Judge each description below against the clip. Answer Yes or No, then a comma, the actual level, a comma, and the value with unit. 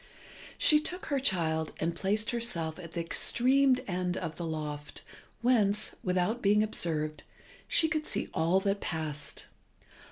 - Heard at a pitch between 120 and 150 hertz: No, medium, 185 Hz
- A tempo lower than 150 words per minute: Yes, average, 140 wpm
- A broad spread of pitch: Yes, wide, 6.6 semitones